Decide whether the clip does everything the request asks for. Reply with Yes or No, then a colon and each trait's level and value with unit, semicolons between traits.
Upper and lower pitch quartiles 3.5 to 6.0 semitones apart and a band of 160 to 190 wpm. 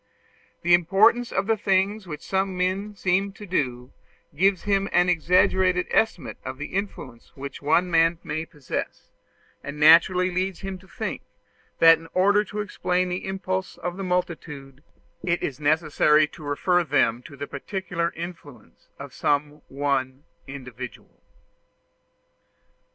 No: average, 4.5 semitones; average, 145 wpm